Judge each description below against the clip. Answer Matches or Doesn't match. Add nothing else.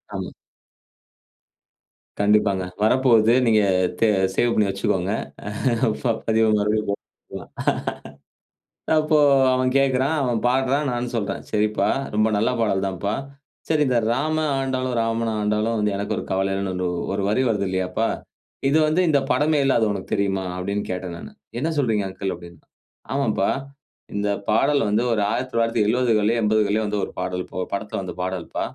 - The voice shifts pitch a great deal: Doesn't match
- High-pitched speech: Doesn't match